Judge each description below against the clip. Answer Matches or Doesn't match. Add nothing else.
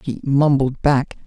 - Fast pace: Doesn't match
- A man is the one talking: Matches